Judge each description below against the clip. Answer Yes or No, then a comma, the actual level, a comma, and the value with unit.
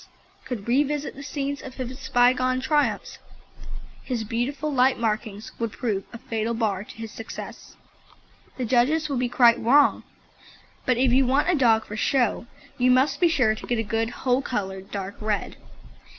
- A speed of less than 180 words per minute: Yes, average, 170 wpm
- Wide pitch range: No, average, 3.1 semitones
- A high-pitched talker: Yes, high, 245 Hz